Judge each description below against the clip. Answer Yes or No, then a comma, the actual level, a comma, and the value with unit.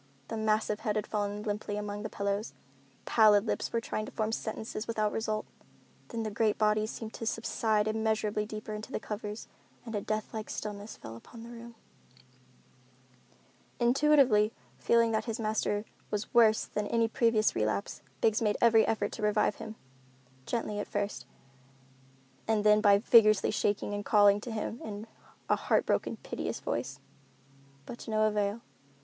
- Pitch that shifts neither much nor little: No, narrow, 1.3 semitones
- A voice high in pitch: Yes, high, 215 Hz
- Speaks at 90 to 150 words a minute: No, average, 165 wpm